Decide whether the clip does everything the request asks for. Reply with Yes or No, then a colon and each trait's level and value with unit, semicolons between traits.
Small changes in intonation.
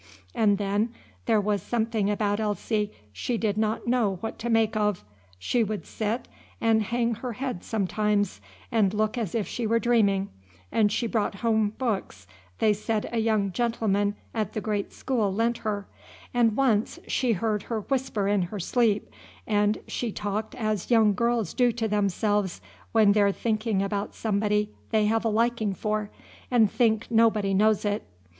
Yes: narrow, 1.9 semitones